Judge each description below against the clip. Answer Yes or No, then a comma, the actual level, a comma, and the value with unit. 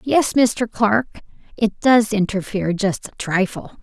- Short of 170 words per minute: Yes, average, 140 wpm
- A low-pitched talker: No, high, 215 Hz